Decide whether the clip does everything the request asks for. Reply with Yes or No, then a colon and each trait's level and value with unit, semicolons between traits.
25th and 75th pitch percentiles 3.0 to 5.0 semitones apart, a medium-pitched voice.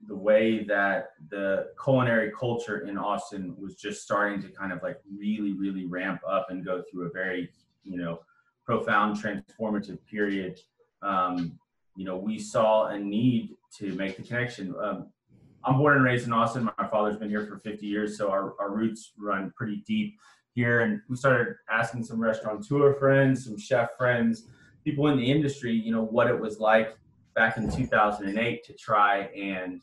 No: average, 3.4 semitones; low, 105 Hz